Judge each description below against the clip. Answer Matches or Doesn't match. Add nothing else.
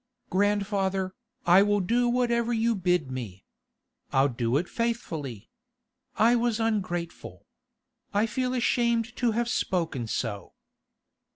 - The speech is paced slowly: Matches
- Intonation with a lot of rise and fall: Matches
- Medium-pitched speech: Doesn't match